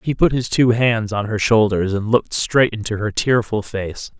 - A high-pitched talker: No, low, 110 Hz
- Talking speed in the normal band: No, fast, 215 wpm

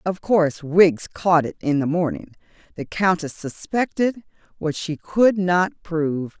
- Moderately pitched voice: Yes, medium, 170 Hz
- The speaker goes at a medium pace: Yes, average, 150 wpm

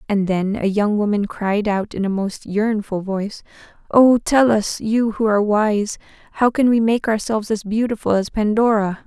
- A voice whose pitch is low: No, high, 210 Hz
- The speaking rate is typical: Yes, average, 185 wpm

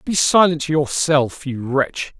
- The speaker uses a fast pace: No, slow, 135 wpm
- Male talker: Yes, male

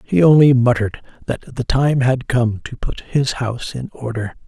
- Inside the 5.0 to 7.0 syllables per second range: No, 4.7 syllables/s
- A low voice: Yes, low, 125 Hz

